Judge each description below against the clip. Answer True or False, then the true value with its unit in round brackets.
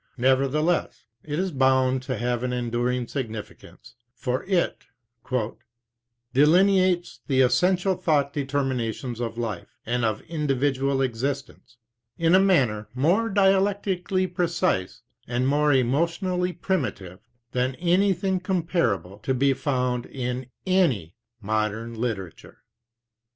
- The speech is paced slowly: True (110 wpm)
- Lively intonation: True (6.5 semitones)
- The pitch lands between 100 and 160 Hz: True (135 Hz)